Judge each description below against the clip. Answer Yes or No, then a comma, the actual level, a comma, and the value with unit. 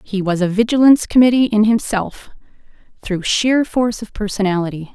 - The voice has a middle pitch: No, high, 215 Hz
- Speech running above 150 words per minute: No, average, 145 wpm